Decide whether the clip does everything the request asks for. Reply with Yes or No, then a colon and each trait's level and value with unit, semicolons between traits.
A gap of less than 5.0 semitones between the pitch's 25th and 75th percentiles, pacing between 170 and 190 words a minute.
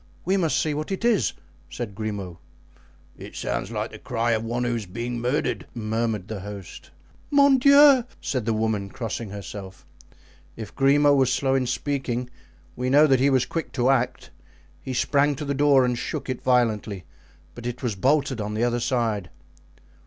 Yes: average, 4.2 semitones; average, 180 wpm